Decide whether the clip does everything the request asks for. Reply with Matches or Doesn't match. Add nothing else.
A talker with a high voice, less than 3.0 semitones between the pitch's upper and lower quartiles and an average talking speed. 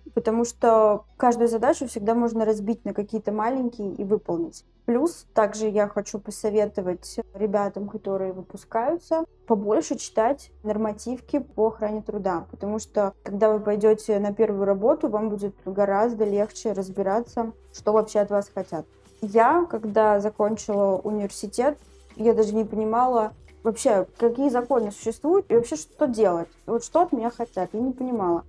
Matches